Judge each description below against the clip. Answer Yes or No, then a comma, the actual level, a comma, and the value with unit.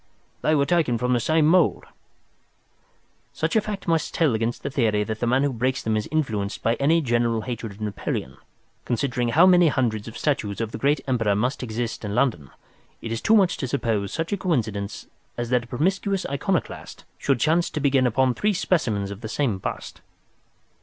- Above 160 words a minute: Yes, average, 195 wpm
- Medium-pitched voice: No, low, 125 Hz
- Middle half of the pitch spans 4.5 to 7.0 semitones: Yes, wide, 5.6 semitones